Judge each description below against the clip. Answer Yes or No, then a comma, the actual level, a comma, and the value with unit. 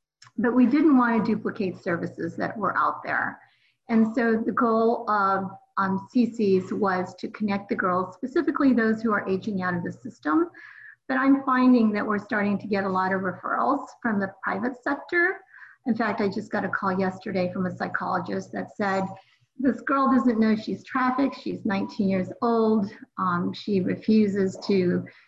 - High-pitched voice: Yes, high, 220 Hz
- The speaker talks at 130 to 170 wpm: No, average, 180 wpm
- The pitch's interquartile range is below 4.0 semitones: No, average, 4.5 semitones